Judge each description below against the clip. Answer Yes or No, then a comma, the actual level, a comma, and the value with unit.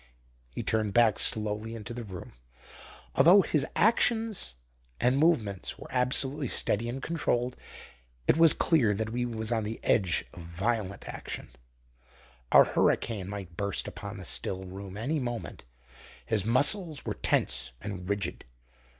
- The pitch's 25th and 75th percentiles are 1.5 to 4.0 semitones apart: No, average, 4.8 semitones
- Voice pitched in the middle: No, low, 110 Hz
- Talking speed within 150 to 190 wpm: No, average, 140 wpm